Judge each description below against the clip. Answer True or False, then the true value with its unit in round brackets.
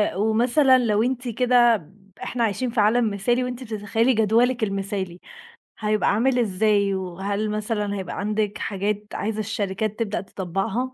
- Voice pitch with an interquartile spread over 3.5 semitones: False (2.9 semitones)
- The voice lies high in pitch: True (215 Hz)